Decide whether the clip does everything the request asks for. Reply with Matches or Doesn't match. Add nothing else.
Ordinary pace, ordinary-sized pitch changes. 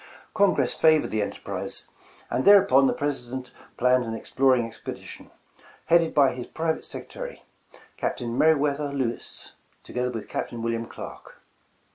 Doesn't match